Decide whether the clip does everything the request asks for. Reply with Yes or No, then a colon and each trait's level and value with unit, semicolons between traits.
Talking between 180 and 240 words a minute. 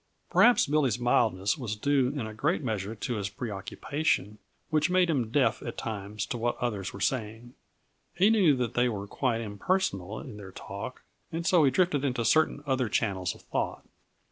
Yes: average, 185 wpm